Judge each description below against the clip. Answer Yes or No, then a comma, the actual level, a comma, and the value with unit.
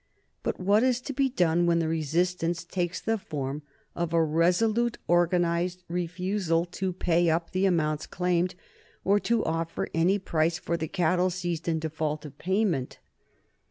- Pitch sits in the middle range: Yes, medium, 175 Hz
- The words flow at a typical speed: Yes, average, 160 wpm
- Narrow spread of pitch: Yes, narrow, 2.1 semitones